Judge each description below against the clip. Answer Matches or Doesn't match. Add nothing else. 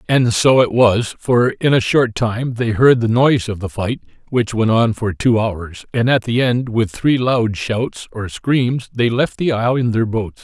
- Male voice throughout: Matches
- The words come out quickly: Matches